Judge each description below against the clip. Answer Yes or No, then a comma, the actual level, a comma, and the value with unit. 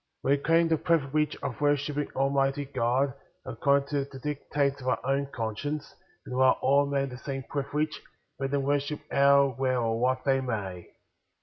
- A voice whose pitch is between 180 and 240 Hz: No, medium, 140 Hz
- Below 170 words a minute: No, average, 180 wpm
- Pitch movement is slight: Yes, narrow, 1.6 semitones